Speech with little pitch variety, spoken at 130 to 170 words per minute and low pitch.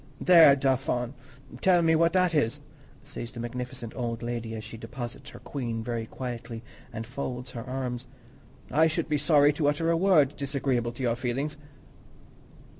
No: average, 3.9 semitones; average, 165 wpm; low, 130 Hz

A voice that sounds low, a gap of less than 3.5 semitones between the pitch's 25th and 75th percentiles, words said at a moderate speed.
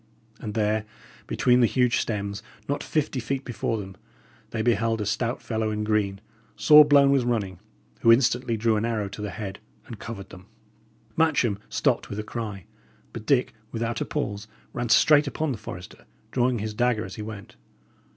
Yes: low, 110 Hz; average, 2.8 semitones; average, 180 wpm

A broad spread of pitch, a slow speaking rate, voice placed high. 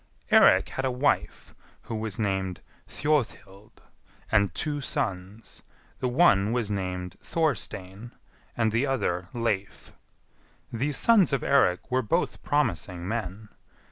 No: wide, 5.7 semitones; slow, 125 wpm; low, 110 Hz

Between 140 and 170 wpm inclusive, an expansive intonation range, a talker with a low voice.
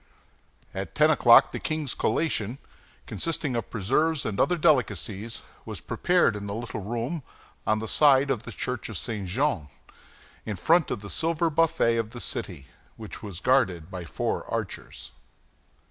Yes: average, 160 wpm; wide, 6.7 semitones; low, 115 Hz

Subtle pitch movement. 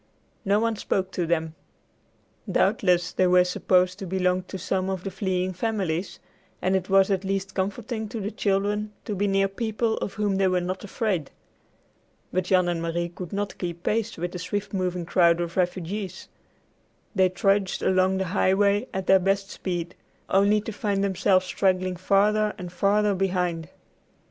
Yes: narrow, 1.9 semitones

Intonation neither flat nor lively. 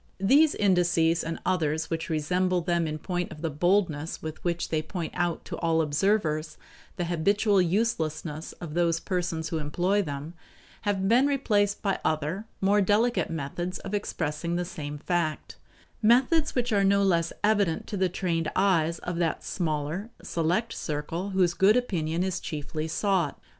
Yes: average, 3.8 semitones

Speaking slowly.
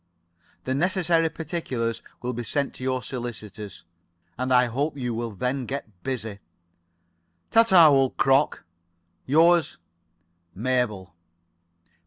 Yes: slow, 115 wpm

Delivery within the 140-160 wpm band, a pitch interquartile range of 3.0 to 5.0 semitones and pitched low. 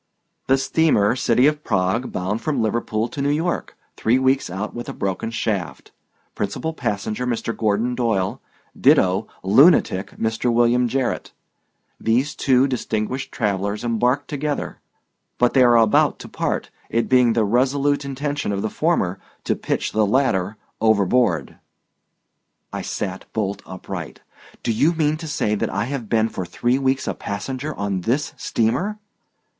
Yes: average, 150 wpm; average, 4.6 semitones; low, 115 Hz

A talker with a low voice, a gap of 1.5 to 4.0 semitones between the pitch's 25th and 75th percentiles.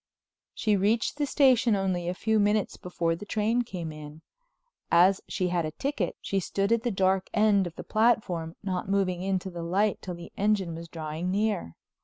No: high, 190 Hz; average, 3.6 semitones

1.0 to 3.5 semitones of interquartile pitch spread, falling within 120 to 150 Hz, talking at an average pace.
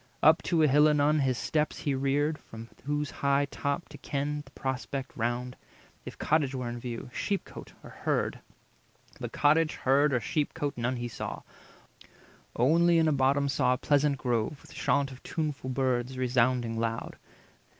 Yes: average, 2.8 semitones; medium, 140 Hz; average, 170 wpm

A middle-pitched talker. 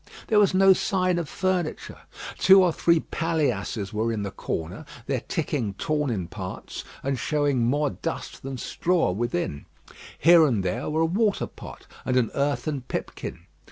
Yes: medium, 145 Hz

